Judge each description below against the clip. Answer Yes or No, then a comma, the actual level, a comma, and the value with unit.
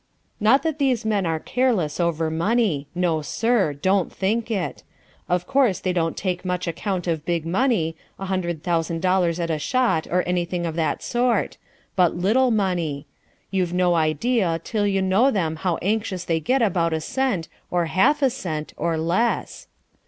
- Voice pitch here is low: No, medium, 180 Hz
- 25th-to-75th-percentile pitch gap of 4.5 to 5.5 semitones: Yes, average, 4.8 semitones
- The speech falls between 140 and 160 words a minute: No, average, 175 wpm